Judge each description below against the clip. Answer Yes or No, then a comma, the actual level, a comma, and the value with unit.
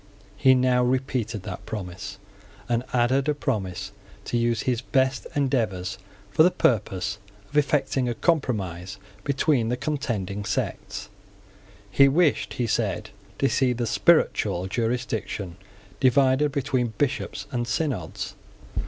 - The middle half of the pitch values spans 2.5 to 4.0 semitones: No, average, 4.6 semitones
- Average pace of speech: No, slow, 125 wpm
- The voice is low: Yes, low, 125 Hz